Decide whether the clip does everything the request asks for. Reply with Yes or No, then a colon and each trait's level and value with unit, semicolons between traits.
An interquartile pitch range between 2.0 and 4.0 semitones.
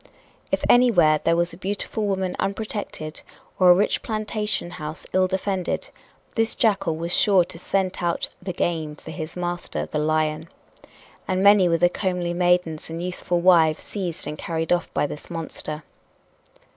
Yes: average, 2.9 semitones